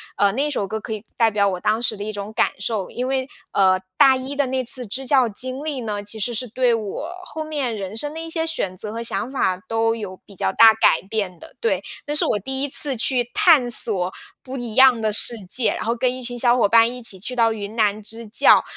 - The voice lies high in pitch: Yes, high, 230 Hz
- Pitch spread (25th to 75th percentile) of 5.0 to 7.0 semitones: No, average, 3.7 semitones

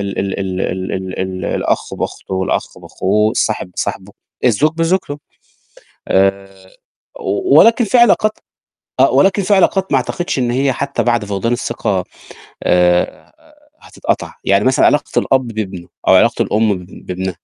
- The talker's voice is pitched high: No, low, 105 Hz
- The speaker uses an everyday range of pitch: No, wide, 6.8 semitones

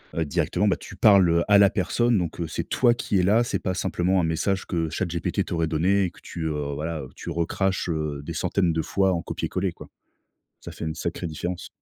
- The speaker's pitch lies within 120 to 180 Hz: No, very low, 85 Hz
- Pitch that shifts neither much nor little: Yes, average, 3.0 semitones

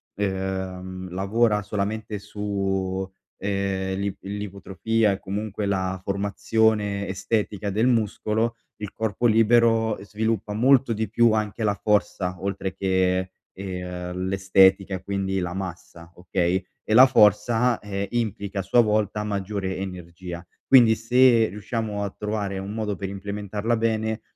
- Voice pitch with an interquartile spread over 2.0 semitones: Yes, narrow, 2.4 semitones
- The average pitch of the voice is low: Yes, low, 100 Hz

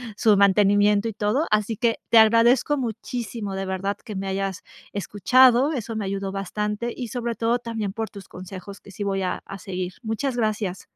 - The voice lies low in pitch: No, high, 210 Hz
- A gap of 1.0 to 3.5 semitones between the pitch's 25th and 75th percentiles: Yes, average, 2.9 semitones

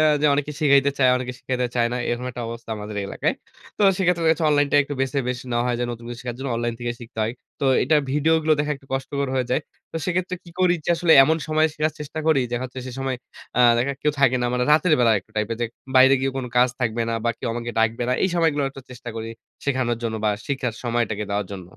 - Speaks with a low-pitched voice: Yes, low, 130 Hz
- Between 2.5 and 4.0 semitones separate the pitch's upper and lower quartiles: Yes, average, 3.7 semitones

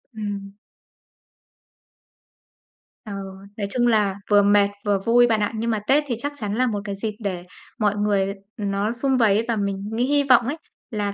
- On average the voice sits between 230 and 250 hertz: No, high, 210 Hz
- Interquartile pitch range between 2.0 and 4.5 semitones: Yes, average, 2.9 semitones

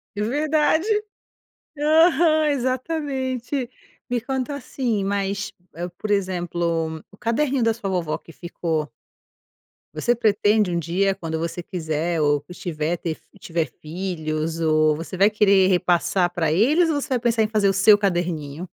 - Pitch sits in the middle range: No, high, 195 Hz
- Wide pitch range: Yes, wide, 6.5 semitones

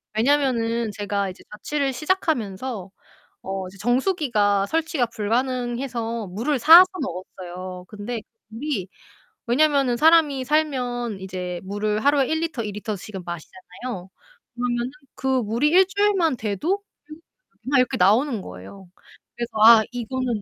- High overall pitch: Yes, high, 235 Hz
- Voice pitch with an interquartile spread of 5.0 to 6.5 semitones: Yes, wide, 5.5 semitones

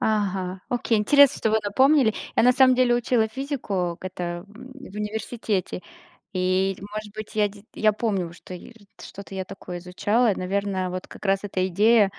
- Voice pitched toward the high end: Yes, high, 205 Hz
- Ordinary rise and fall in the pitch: Yes, average, 3.6 semitones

